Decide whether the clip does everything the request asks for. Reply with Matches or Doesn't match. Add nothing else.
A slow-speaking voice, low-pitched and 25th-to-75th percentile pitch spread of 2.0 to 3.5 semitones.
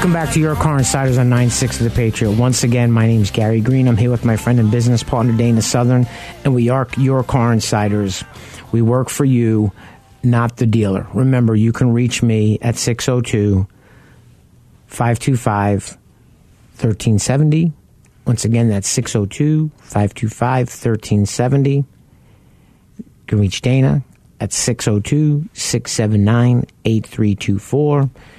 Matches